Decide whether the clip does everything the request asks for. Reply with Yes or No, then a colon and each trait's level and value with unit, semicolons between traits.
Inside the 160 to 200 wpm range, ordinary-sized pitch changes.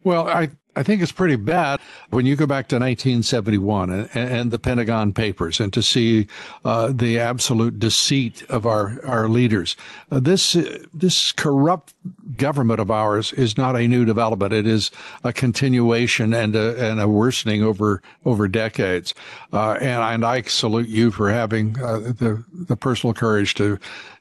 Yes: average, 170 wpm; average, 3.1 semitones